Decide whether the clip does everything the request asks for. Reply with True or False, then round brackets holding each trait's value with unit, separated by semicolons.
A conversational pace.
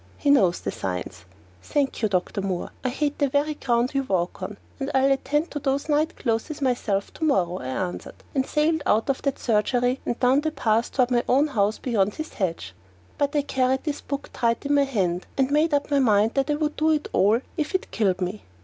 False (230 wpm)